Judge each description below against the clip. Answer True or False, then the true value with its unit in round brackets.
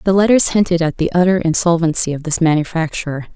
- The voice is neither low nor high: True (170 Hz)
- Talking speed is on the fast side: False (180 wpm)